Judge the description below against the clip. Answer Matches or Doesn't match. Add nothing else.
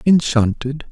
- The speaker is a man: Matches